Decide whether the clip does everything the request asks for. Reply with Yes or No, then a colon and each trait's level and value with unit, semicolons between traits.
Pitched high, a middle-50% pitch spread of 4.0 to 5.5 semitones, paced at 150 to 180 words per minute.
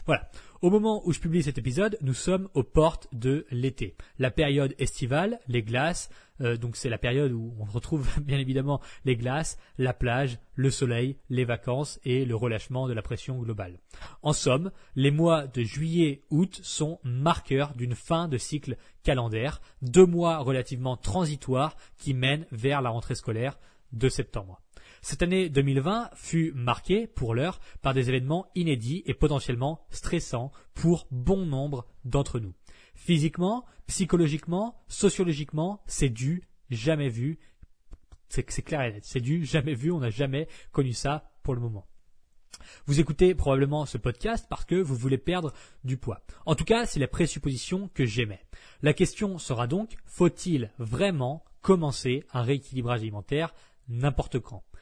No: medium, 140 Hz; average, 4.7 semitones; average, 160 wpm